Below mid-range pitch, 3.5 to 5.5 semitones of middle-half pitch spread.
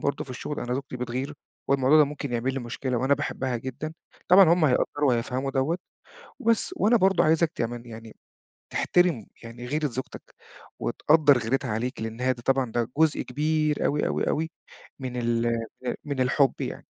Yes: low, 130 Hz; average, 3.9 semitones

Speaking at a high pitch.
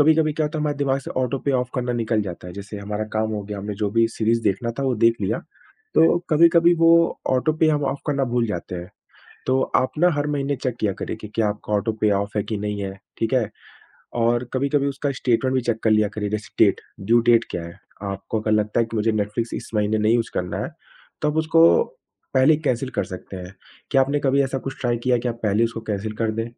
No: low, 115 Hz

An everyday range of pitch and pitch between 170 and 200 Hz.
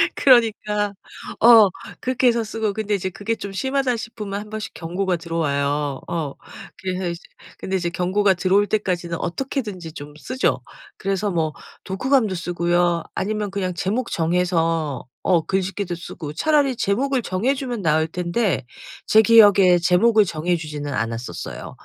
Yes: average, 4.3 semitones; high, 190 Hz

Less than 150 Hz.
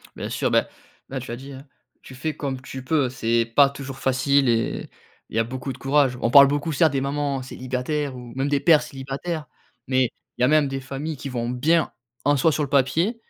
Yes: low, 135 Hz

